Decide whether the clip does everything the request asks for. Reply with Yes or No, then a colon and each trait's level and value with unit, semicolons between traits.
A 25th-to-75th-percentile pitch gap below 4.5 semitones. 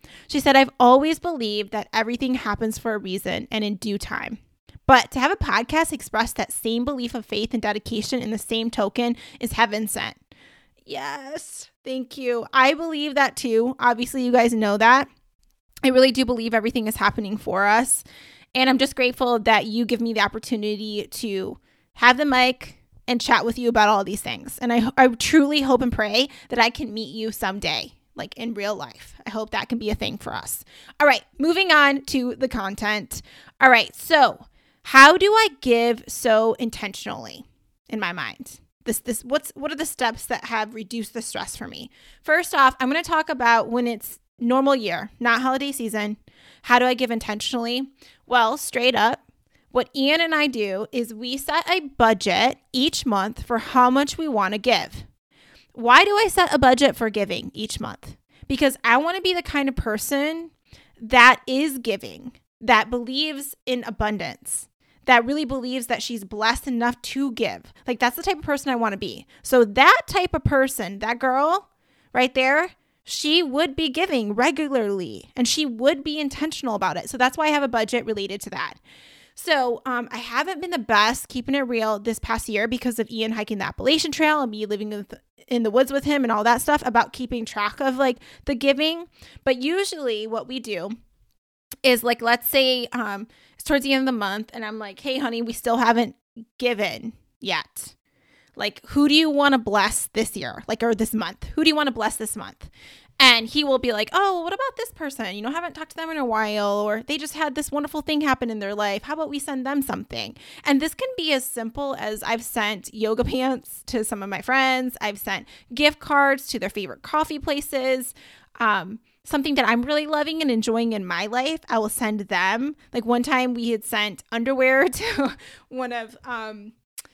Yes: average, 3.9 semitones